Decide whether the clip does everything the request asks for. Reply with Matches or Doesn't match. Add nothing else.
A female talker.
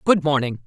Matches